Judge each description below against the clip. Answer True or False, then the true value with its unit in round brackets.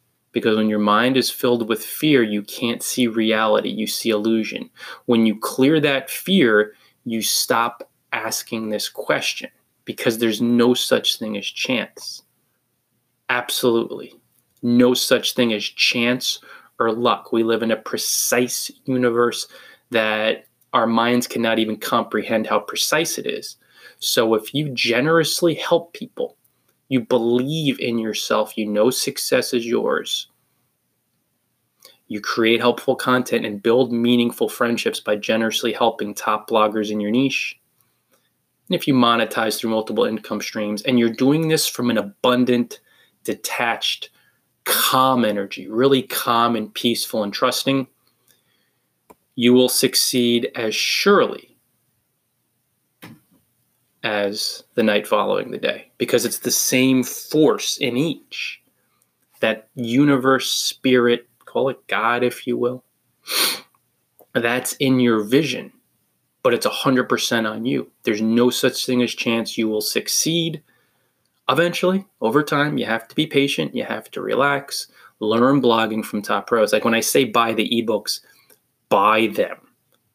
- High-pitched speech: False (120 Hz)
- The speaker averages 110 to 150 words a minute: True (140 wpm)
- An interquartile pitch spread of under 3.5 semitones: True (2.4 semitones)